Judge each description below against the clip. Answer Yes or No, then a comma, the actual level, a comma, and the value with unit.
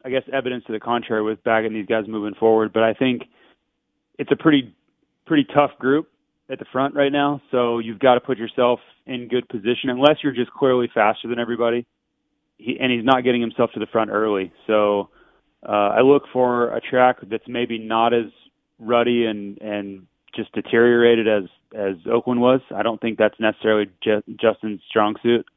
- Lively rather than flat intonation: No, narrow, 2.6 semitones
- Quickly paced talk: No, average, 190 wpm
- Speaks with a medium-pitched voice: No, low, 120 Hz